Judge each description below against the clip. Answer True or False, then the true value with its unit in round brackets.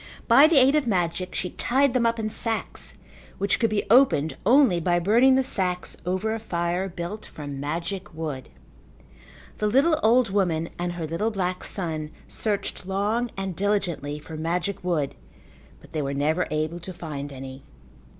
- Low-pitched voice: False (185 Hz)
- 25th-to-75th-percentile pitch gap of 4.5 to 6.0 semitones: True (5.2 semitones)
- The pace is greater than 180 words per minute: False (170 wpm)